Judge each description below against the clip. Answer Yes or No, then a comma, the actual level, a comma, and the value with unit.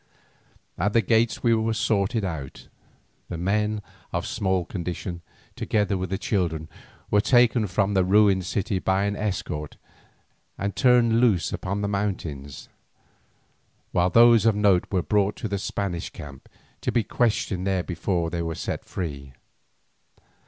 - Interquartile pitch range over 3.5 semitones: No, average, 3.2 semitones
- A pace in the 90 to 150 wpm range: Yes, average, 145 wpm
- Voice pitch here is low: Yes, low, 100 Hz